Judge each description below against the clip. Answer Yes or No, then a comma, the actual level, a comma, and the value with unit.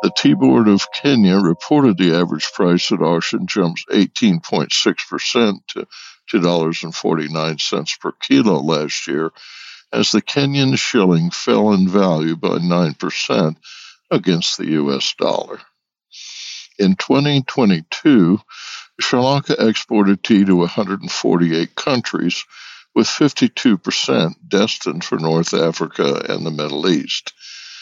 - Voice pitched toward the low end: Yes, very low, 90 Hz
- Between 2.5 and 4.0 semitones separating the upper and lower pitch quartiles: No, average, 4.6 semitones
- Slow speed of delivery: Yes, slow, 110 wpm